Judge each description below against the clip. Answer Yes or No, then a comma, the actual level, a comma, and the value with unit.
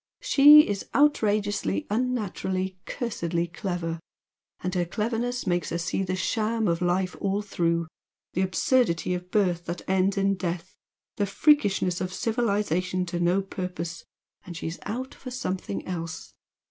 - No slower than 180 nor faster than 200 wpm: No, average, 140 wpm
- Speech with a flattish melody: No, average, 3.3 semitones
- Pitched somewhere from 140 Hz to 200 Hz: Yes, medium, 185 Hz